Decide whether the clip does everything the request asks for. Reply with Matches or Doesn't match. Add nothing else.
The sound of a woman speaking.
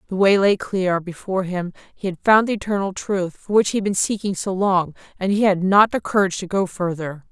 Matches